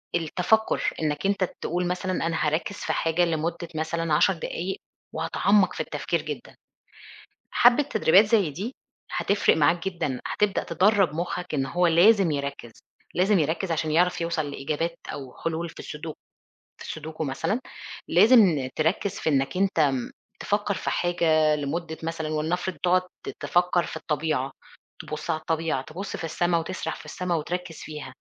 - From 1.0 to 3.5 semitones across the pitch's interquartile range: Yes, average, 2.8 semitones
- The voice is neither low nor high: Yes, medium, 165 Hz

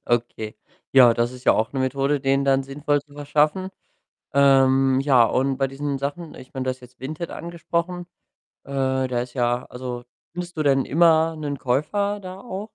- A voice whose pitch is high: No, low, 135 Hz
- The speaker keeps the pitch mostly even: No, average, 3.2 semitones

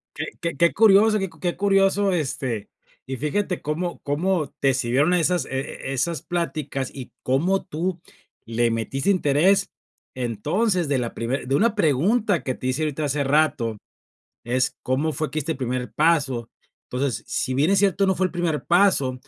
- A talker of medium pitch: Yes, medium, 150 Hz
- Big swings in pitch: Yes, wide, 5.7 semitones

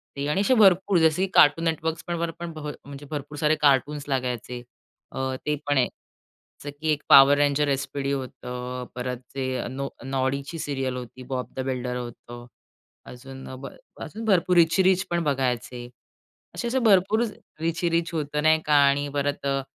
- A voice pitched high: No, medium, 145 Hz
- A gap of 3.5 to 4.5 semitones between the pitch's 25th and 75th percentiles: Yes, average, 3.8 semitones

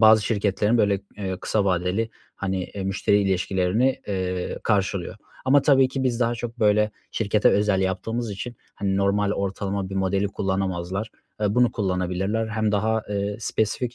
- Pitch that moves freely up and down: No, narrow, 2.6 semitones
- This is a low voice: Yes, low, 100 Hz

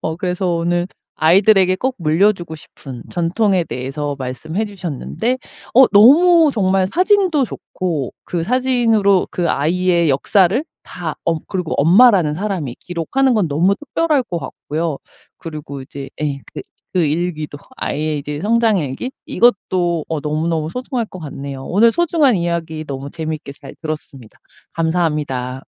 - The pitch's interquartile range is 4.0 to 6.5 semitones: Yes, wide, 5.6 semitones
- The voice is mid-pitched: Yes, medium, 175 Hz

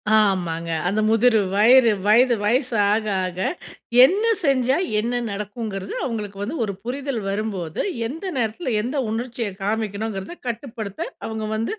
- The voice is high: Yes, high, 220 Hz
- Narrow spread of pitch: No, average, 3.4 semitones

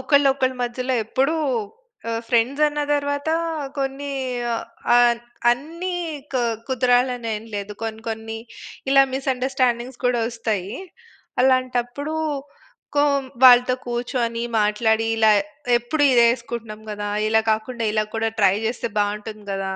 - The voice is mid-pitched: No, high, 240 Hz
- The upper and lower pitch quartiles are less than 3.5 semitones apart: Yes, average, 2.8 semitones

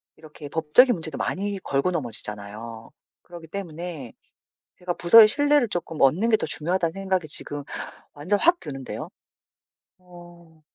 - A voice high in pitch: No, medium, 170 Hz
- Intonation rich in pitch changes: No, average, 4.8 semitones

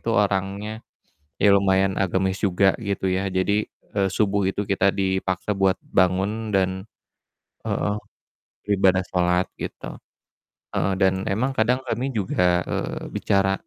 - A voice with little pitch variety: Yes, narrow, 1.5 semitones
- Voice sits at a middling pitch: No, very low, 95 Hz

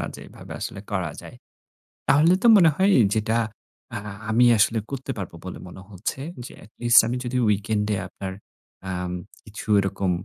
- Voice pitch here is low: Yes, low, 110 Hz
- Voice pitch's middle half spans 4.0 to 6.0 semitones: Yes, average, 4.4 semitones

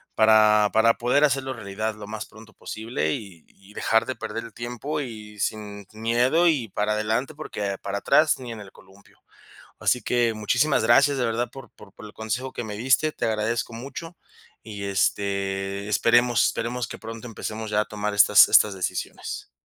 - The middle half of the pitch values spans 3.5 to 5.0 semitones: No, average, 2.7 semitones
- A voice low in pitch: Yes, low, 110 Hz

